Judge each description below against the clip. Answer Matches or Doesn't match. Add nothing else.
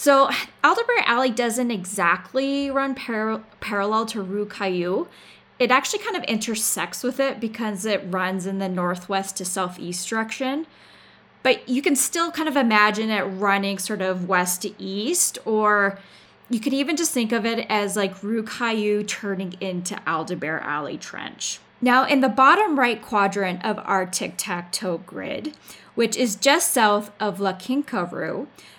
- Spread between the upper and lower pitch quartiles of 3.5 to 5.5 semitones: Matches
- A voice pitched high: Matches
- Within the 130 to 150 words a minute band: Doesn't match